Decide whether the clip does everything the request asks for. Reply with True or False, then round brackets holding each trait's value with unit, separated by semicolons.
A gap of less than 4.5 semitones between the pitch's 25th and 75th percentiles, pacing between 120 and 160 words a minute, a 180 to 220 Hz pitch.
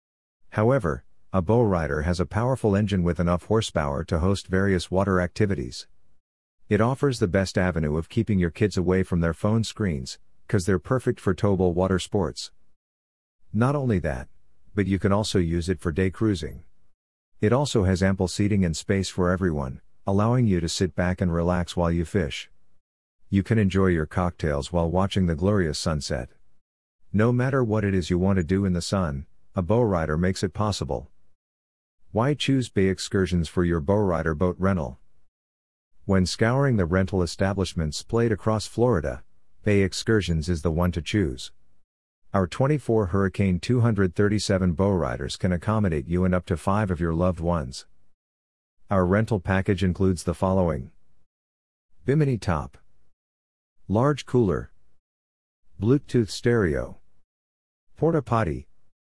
False (4.0 semitones; 155 wpm; 95 Hz)